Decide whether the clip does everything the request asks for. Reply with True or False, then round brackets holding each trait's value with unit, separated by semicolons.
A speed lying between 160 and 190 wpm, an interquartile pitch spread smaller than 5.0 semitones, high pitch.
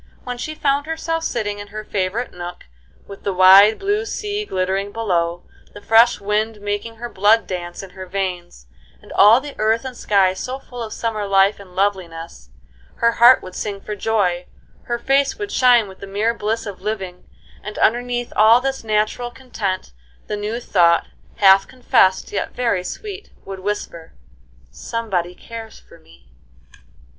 True (165 wpm; 4.0 semitones; 210 Hz)